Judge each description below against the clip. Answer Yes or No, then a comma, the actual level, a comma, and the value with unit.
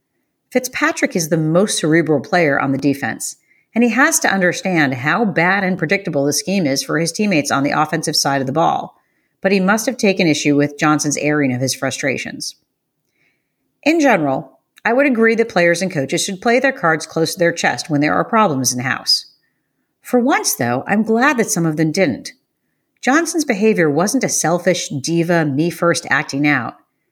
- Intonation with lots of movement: Yes, wide, 7.0 semitones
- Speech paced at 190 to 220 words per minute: Yes, average, 195 wpm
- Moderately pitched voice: Yes, medium, 170 Hz